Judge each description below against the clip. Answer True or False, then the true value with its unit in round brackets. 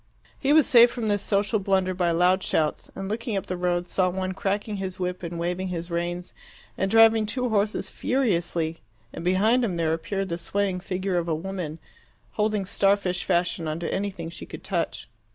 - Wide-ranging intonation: False (2.7 semitones)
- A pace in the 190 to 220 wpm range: True (195 wpm)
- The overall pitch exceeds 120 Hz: True (185 Hz)